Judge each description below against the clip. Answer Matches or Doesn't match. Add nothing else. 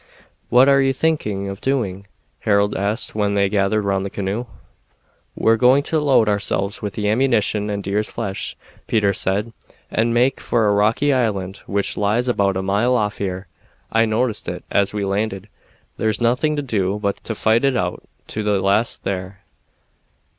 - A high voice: Doesn't match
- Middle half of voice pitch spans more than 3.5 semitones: Doesn't match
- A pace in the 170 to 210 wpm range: Matches